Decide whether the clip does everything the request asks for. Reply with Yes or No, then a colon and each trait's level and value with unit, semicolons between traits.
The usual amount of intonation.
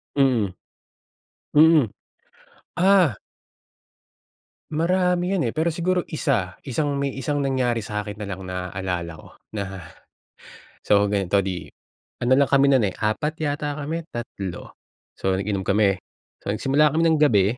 No: wide, 7.5 semitones